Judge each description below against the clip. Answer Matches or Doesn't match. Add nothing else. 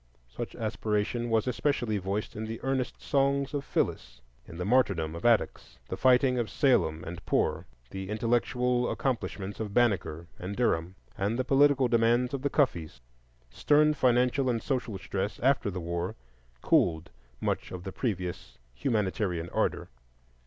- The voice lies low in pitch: Matches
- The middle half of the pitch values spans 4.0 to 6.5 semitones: Matches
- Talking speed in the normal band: Matches